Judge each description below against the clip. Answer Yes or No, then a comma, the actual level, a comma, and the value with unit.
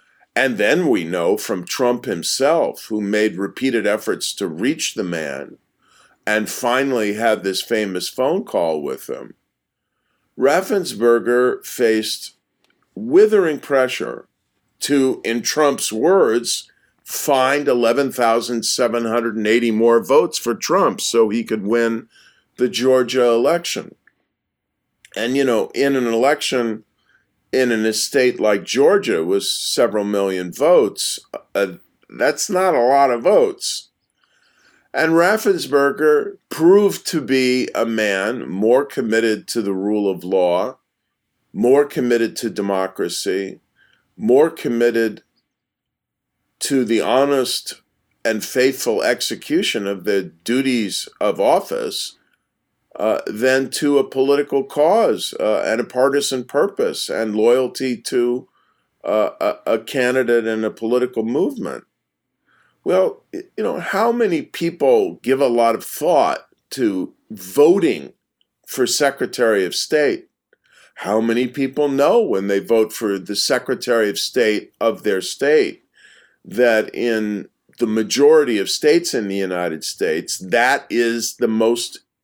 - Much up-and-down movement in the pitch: Yes, wide, 7.0 semitones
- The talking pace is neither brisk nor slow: No, slow, 120 wpm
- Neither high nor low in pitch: No, low, 125 Hz